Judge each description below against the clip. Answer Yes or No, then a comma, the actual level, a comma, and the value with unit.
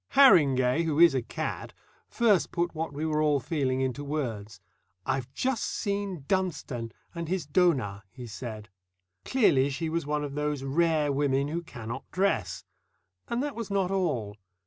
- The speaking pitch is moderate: Yes, medium, 150 Hz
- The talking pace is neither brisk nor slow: Yes, average, 160 wpm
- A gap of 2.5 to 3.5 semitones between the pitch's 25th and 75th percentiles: No, average, 4.9 semitones